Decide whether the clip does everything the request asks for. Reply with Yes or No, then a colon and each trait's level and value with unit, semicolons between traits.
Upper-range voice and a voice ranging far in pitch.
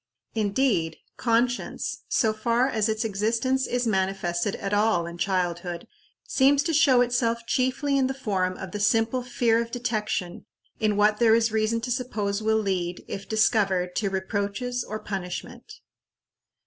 No: high, 220 Hz; average, 3.8 semitones